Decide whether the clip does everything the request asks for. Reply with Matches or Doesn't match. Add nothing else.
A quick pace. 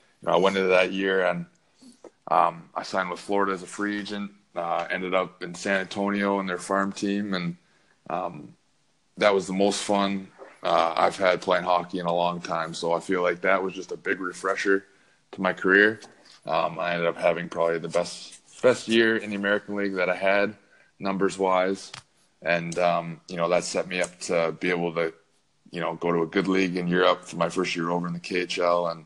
Matches